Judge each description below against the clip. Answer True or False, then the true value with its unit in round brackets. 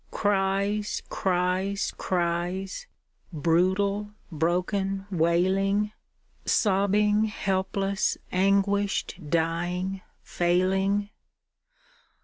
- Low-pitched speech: False (190 Hz)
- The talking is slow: True (55 wpm)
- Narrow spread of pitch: True (2.0 semitones)